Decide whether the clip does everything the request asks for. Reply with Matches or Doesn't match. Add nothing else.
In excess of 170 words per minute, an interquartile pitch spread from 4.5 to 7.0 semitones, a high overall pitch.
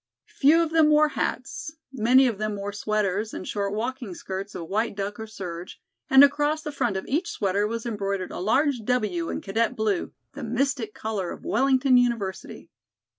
Matches